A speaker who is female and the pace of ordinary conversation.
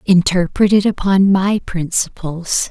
No: female; slow, 110 wpm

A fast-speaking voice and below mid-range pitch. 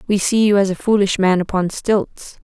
No: fast, 220 wpm; high, 195 Hz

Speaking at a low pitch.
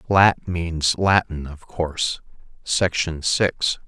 Yes: very low, 85 Hz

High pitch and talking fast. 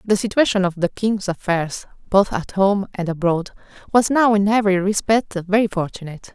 No: high, 195 Hz; average, 170 wpm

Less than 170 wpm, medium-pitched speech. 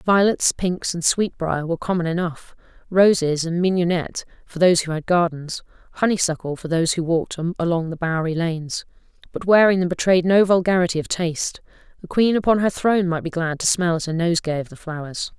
No: average, 185 wpm; medium, 175 Hz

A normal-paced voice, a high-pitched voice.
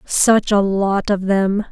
Yes: average, 175 wpm; high, 200 Hz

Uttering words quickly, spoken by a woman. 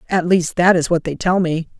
Yes: fast, 270 wpm; female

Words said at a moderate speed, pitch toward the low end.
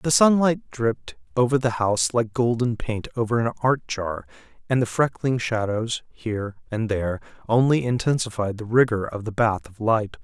Yes: average, 170 wpm; low, 115 Hz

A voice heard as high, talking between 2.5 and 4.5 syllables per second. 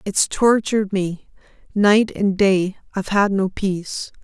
Yes: high, 200 Hz; 4.2 syllables/s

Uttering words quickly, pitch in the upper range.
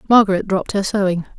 No: average, 175 wpm; high, 195 Hz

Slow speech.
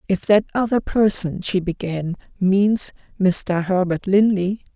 Yes: slow, 125 wpm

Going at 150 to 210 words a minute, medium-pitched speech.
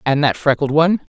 Yes: fast, 205 wpm; medium, 155 Hz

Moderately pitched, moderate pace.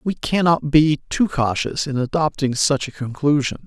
Yes: medium, 145 Hz; average, 165 wpm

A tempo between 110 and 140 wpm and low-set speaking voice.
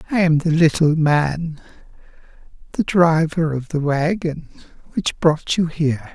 No: slow, 135 wpm; medium, 160 Hz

